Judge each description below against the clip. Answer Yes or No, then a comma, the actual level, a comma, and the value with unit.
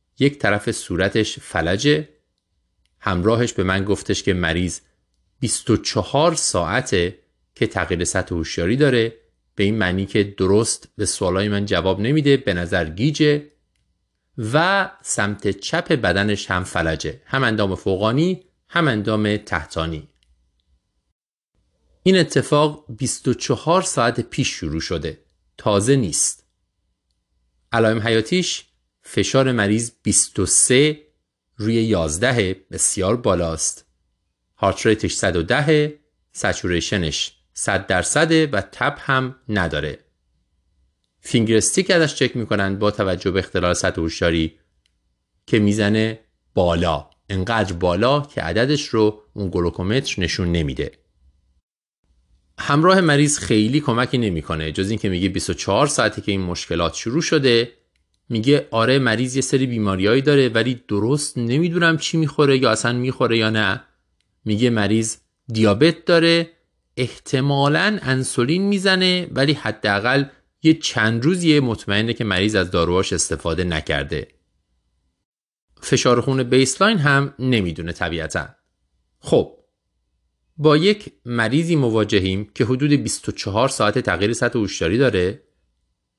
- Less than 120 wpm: Yes, average, 110 wpm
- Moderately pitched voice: No, low, 110 Hz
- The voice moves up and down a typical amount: No, wide, 7.1 semitones